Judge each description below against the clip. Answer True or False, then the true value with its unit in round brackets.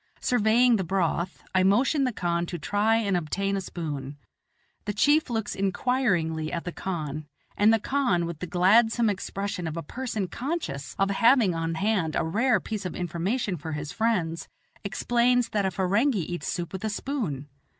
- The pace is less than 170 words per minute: False (175 wpm)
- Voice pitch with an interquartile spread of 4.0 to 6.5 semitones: True (5.0 semitones)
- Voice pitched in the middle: False (195 Hz)